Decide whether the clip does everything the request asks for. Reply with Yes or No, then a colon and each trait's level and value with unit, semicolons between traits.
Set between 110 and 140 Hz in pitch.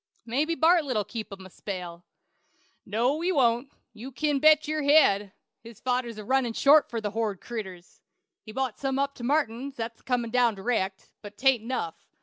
No: high, 240 Hz